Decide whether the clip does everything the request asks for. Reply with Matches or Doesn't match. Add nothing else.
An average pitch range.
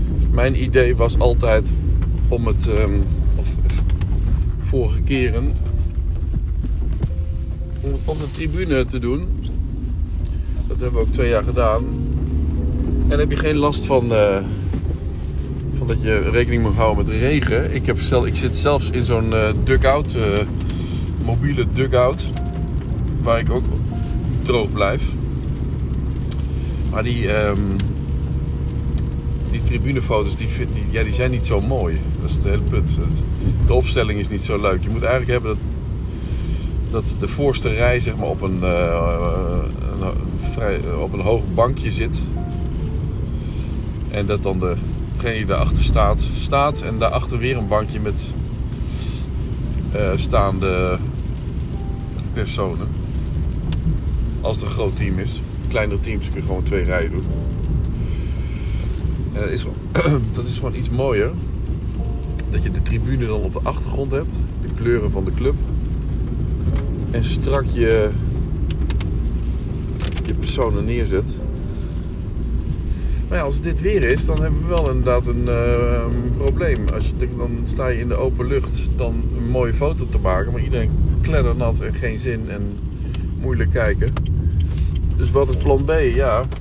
Doesn't match